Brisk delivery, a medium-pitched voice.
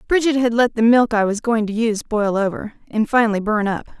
No: fast, 240 wpm; high, 225 Hz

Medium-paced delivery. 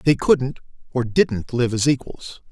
Yes: average, 165 wpm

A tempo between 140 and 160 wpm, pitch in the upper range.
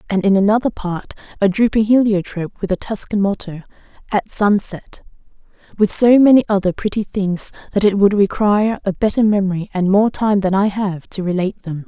No: average, 170 wpm; high, 200 Hz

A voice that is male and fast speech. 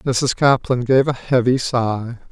No: male; average, 155 wpm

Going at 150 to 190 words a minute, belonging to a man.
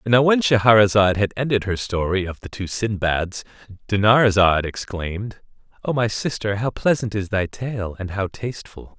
Yes: average, 160 wpm; male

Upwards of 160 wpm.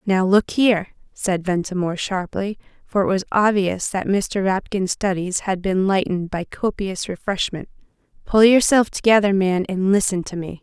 No: average, 145 wpm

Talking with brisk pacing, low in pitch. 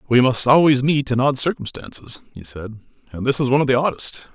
Yes: fast, 220 wpm; low, 130 Hz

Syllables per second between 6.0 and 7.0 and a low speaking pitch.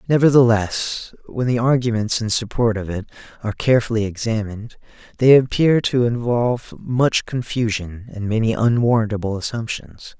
No: 5.1 syllables/s; low, 115 Hz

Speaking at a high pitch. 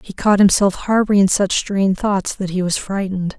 Yes: high, 195 Hz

